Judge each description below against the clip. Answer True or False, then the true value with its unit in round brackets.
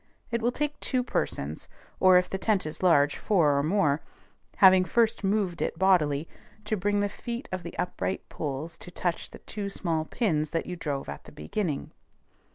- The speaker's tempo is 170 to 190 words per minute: True (185 wpm)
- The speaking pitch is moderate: True (180 Hz)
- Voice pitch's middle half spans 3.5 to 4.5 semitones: False (4.9 semitones)